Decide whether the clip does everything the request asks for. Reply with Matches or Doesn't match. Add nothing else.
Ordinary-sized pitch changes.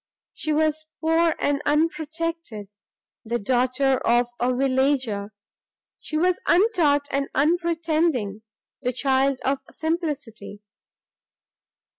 Matches